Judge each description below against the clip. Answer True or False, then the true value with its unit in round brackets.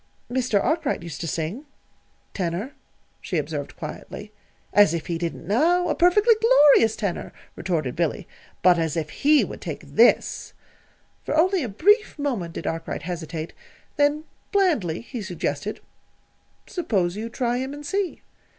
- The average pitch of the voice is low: False (220 Hz)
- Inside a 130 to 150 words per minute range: True (145 wpm)